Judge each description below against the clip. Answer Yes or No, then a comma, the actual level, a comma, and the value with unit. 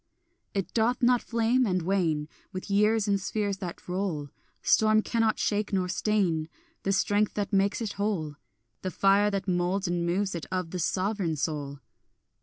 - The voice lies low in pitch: No, high, 195 Hz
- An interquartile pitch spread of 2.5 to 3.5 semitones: Yes, average, 3.0 semitones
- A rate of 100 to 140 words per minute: No, average, 165 wpm